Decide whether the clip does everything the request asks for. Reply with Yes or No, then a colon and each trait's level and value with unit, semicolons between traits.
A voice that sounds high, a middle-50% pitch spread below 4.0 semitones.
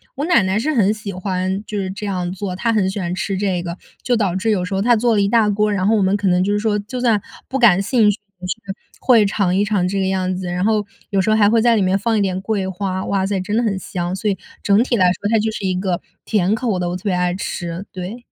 Yes: high, 200 Hz; narrow, 2.6 semitones